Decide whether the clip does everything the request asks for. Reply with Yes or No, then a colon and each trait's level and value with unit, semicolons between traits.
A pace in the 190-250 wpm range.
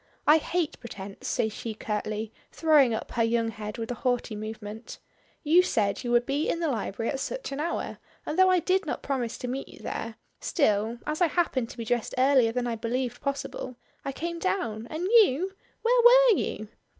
Yes: average, 200 wpm